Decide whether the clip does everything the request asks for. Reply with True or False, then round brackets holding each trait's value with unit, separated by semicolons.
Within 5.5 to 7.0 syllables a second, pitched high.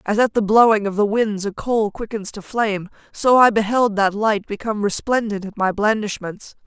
False (5.1 syllables/s; 210 Hz)